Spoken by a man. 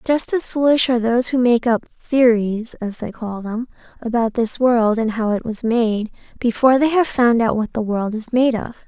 No: female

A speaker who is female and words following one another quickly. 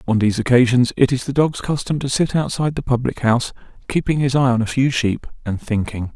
No: male; fast, 225 wpm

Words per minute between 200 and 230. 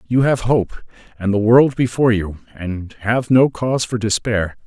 No: average, 180 wpm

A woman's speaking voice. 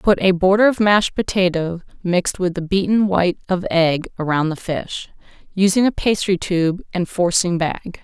Yes: female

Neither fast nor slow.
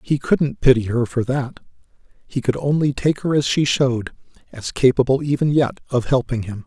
Yes: average, 180 wpm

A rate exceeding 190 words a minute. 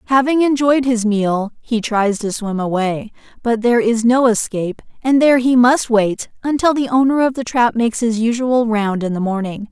Yes: average, 200 wpm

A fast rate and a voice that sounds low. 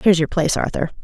No: fast, 230 wpm; medium, 170 Hz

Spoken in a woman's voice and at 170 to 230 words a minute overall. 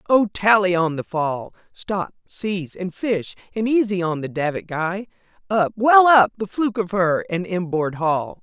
Yes: female; average, 180 wpm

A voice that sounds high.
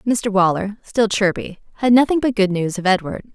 Yes: high, 205 Hz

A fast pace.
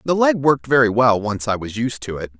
Yes: fast, 275 wpm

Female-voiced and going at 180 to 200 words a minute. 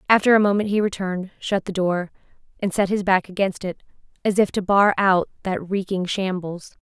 Yes: female; average, 195 wpm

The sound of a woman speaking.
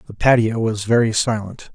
No: male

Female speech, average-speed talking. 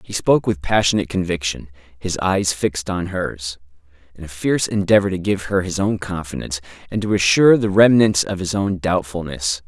No: male; average, 180 wpm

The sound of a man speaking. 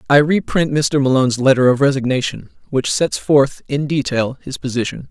Yes: male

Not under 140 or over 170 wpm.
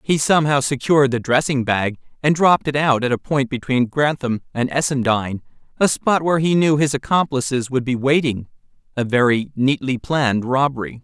Yes: average, 165 wpm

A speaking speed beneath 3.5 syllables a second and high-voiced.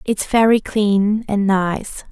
Yes: 3.1 syllables/s; high, 205 Hz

